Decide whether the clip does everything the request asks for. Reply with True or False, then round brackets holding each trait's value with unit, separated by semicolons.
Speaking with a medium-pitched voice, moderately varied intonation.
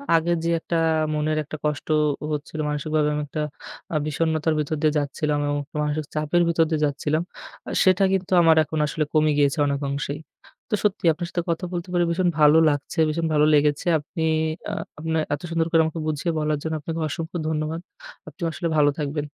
False (155 Hz; 1.9 semitones)